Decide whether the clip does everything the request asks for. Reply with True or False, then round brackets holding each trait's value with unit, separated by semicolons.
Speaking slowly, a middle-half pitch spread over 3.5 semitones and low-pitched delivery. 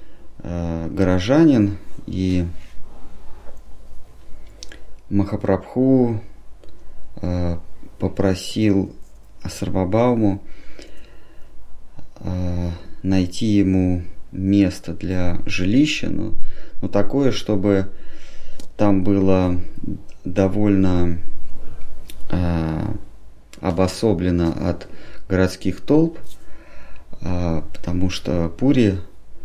False (50 wpm; 2.7 semitones; 95 Hz)